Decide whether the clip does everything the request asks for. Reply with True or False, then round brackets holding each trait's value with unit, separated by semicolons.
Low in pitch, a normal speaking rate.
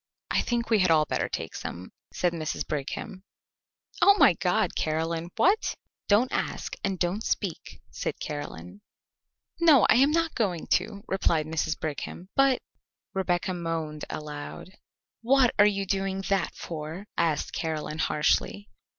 False (180 Hz; 150 wpm)